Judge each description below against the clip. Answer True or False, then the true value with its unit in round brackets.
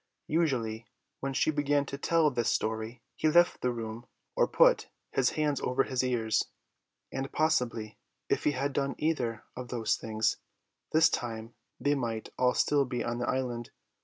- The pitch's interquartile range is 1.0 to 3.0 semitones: False (3.8 semitones)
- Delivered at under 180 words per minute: True (165 wpm)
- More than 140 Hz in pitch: False (125 Hz)